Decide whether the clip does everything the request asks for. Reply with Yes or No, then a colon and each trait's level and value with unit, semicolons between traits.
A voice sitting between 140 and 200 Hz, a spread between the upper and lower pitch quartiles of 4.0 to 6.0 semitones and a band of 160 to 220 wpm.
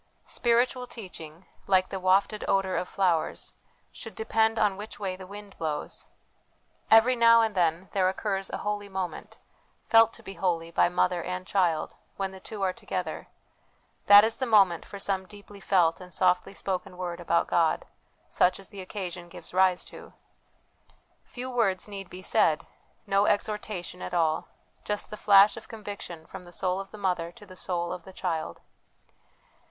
No: high, 190 Hz; narrow, 2.6 semitones; average, 170 wpm